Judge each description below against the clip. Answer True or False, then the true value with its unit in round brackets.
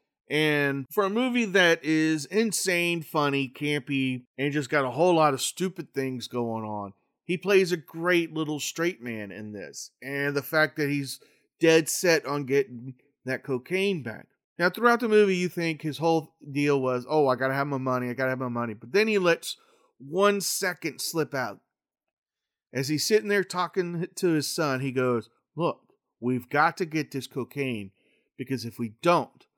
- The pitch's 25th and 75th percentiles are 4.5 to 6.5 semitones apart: True (4.9 semitones)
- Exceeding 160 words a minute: True (190 wpm)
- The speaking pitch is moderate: True (150 Hz)